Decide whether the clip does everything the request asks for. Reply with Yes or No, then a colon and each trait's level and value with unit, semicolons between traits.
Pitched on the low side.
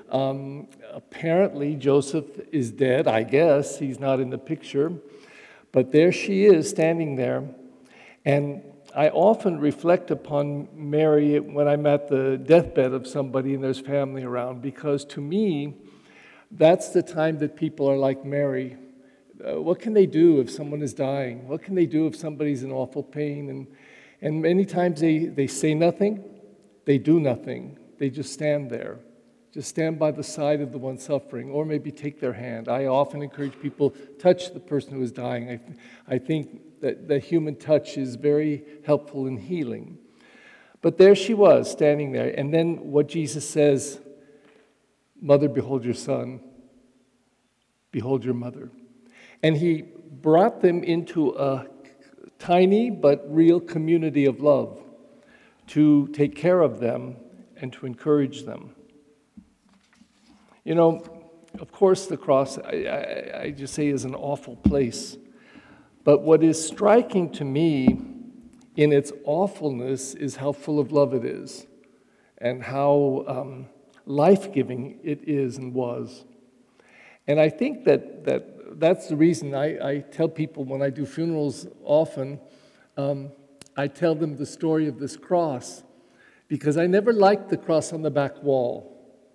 No: medium, 145 Hz